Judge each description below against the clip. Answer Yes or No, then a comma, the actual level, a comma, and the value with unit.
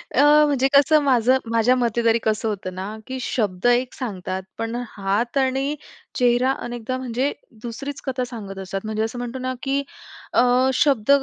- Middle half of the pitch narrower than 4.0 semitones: Yes, average, 3.2 semitones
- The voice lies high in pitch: Yes, high, 240 Hz